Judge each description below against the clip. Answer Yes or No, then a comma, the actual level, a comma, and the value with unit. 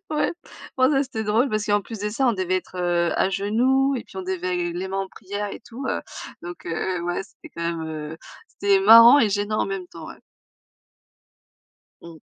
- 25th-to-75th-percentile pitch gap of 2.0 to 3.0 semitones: No, average, 4.2 semitones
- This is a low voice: No, high, 195 Hz